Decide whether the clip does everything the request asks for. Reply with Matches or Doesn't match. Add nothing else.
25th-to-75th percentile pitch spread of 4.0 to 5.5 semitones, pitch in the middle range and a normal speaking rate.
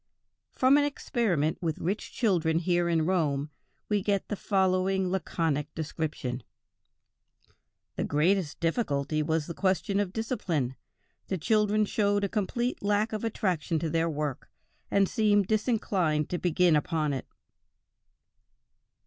Doesn't match